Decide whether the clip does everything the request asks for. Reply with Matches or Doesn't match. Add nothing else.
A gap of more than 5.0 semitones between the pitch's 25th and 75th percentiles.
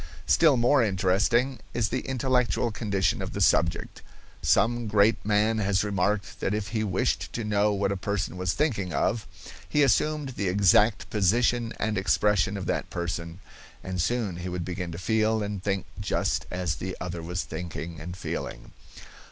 Doesn't match